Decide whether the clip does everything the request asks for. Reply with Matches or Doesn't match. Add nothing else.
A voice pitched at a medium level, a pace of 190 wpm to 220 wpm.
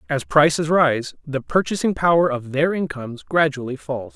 Doesn't match